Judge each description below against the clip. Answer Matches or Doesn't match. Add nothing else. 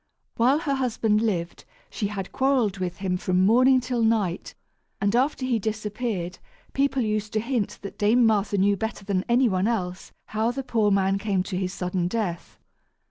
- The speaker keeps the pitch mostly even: Doesn't match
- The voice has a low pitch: Doesn't match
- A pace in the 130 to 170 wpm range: Doesn't match